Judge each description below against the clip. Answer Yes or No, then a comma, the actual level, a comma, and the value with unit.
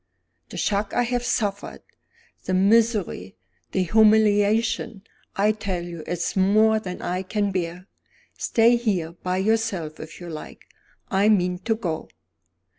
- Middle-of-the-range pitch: No, high, 200 Hz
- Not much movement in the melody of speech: No, average, 3.4 semitones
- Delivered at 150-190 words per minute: No, slow, 135 wpm